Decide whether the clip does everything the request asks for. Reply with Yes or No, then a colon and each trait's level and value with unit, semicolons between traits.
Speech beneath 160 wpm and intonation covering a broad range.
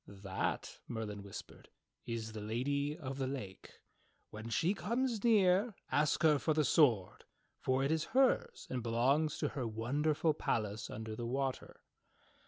Yes: average, 150 wpm; wide, 5.9 semitones